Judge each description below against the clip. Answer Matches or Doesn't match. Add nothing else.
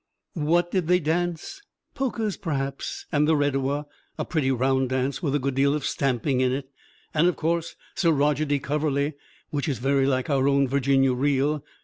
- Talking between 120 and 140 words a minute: Doesn't match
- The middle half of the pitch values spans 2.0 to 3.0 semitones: Matches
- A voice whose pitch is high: Doesn't match